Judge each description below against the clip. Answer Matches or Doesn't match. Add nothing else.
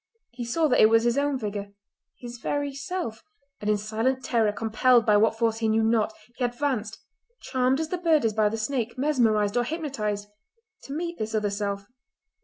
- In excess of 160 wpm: Matches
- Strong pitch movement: Doesn't match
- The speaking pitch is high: Matches